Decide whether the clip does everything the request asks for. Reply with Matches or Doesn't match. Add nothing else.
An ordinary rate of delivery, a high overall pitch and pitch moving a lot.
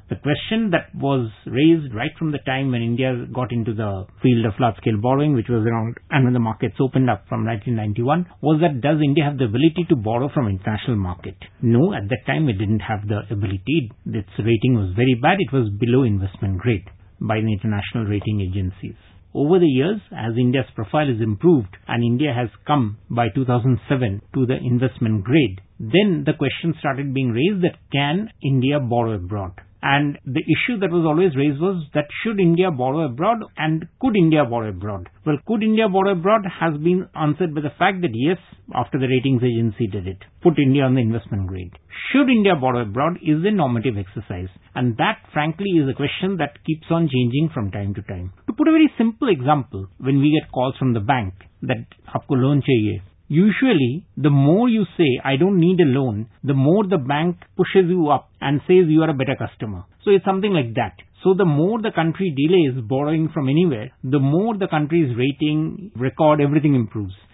Doesn't match